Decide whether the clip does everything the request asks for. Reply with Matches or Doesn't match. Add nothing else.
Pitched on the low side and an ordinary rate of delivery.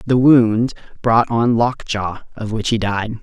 Matches